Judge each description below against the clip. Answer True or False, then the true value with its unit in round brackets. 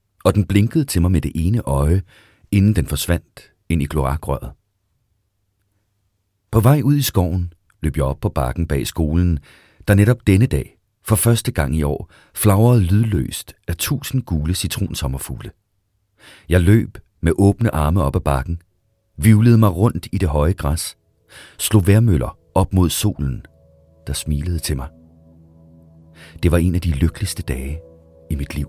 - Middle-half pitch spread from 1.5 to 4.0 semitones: False (4.5 semitones)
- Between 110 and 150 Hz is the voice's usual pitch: False (90 Hz)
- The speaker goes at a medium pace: True (160 wpm)